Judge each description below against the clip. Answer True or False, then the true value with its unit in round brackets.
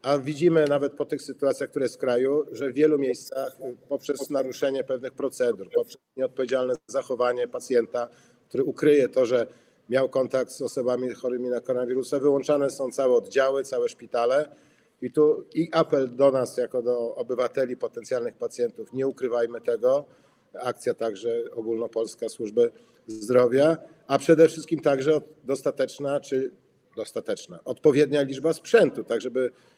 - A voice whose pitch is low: False (145 Hz)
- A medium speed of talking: True (140 wpm)